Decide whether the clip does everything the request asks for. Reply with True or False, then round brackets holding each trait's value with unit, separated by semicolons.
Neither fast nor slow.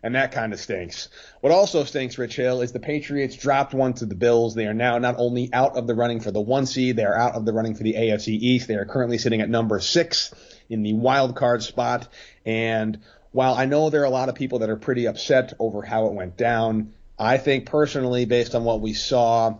False (240 wpm)